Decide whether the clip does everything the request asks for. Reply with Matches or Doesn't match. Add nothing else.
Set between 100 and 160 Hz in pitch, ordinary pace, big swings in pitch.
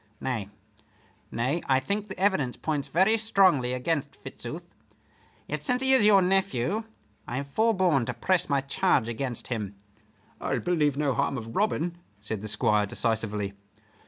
Matches